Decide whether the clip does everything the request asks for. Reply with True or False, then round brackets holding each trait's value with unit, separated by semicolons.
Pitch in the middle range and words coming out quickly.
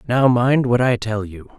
False (120 Hz; 225 wpm)